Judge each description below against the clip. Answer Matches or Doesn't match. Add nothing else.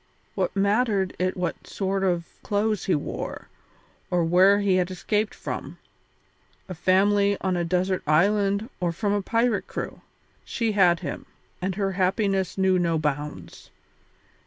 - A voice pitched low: Doesn't match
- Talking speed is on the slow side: Doesn't match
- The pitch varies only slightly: Matches